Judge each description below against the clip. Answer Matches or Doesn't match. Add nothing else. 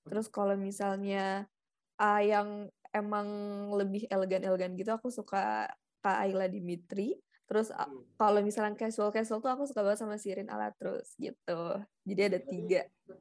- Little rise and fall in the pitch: Matches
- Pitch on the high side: Matches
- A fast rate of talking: Doesn't match